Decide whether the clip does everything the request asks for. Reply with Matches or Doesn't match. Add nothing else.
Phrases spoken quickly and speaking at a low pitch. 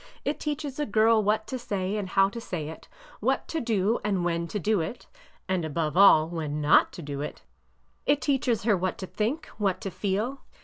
Doesn't match